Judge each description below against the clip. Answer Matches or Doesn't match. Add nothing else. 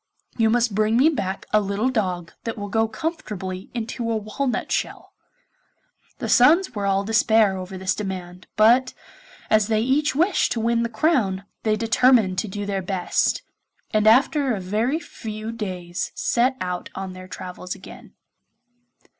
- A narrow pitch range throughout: Doesn't match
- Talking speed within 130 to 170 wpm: Matches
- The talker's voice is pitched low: Doesn't match